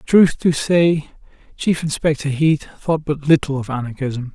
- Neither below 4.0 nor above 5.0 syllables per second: Yes, 4.4 syllables/s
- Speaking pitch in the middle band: Yes, medium, 150 Hz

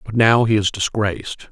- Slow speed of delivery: No, average, 200 wpm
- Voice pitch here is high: No, low, 105 Hz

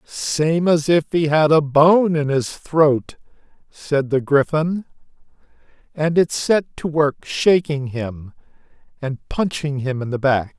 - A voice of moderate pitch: Yes, medium, 150 Hz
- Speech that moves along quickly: No, average, 145 wpm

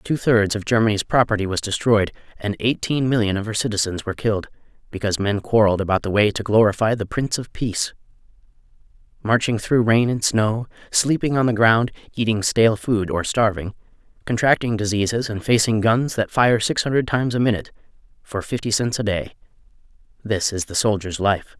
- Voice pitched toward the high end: No, low, 110 Hz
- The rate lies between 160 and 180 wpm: Yes, average, 170 wpm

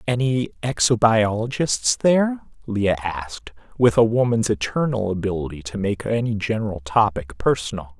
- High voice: No, low, 110 Hz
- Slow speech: Yes, slow, 120 wpm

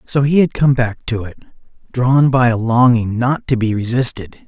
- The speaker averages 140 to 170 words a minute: No, average, 200 wpm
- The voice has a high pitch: No, low, 120 Hz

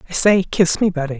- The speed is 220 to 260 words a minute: Yes, fast, 250 wpm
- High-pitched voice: Yes, high, 200 Hz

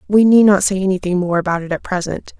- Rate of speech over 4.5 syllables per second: Yes, 6.3 syllables/s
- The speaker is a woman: Yes, female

